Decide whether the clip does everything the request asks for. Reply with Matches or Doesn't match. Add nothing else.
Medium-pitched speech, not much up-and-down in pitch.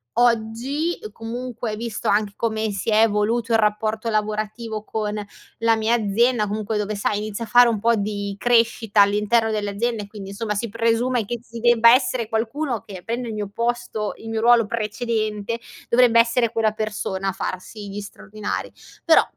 Doesn't match